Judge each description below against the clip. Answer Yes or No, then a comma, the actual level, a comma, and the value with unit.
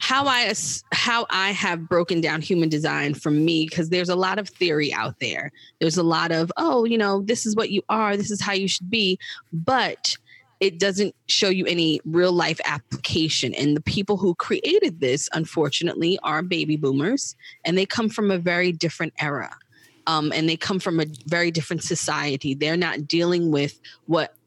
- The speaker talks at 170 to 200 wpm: Yes, average, 190 wpm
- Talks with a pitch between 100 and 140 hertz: No, medium, 175 Hz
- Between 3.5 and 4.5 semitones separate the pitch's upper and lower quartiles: Yes, average, 3.9 semitones